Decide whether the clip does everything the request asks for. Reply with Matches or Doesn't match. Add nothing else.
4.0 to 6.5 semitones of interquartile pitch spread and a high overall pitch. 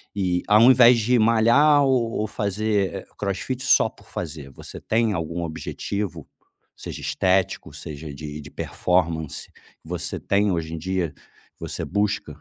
Doesn't match